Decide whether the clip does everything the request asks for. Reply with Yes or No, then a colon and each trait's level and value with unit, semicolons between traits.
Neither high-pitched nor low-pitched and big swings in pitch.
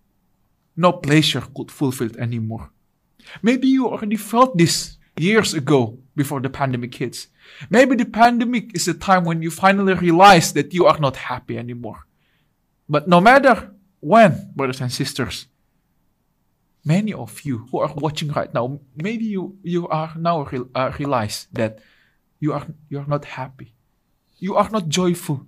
Yes: medium, 155 Hz; wide, 6.1 semitones